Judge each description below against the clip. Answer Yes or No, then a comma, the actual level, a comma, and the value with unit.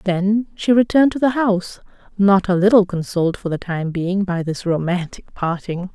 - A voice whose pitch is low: No, high, 190 Hz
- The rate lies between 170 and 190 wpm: Yes, average, 180 wpm